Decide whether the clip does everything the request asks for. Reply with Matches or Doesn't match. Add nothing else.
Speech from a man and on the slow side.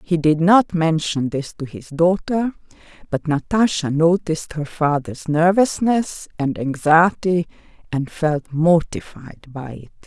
Doesn't match